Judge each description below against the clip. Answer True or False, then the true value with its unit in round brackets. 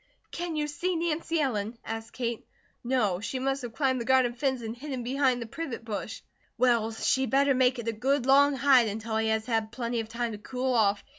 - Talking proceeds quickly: True (215 wpm)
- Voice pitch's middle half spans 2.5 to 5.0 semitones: True (3.3 semitones)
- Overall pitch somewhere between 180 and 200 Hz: False (245 Hz)